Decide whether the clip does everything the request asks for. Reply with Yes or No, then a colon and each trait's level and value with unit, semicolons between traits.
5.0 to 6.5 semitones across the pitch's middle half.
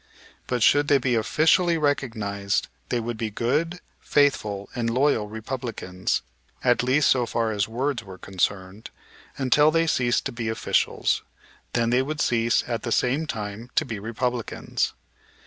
No: average, 4.1 semitones